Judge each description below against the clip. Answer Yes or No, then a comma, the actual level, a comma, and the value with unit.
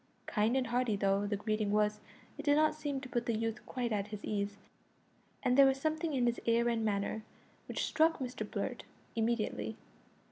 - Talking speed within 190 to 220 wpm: Yes, average, 200 wpm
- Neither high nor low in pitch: No, high, 230 Hz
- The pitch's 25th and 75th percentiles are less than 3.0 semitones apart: No, average, 3.9 semitones